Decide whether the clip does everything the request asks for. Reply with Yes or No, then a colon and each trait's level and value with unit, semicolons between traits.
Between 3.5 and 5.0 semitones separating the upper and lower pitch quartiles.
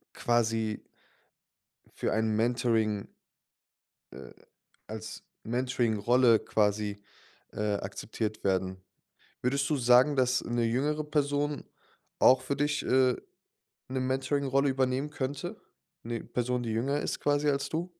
Yes: average, 3.9 semitones